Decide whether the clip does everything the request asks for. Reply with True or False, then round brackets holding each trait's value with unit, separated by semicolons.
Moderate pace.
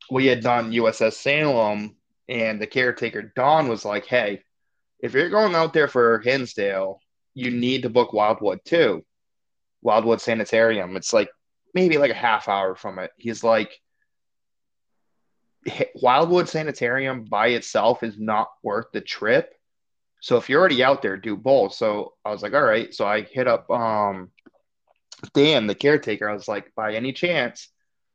True (160 wpm)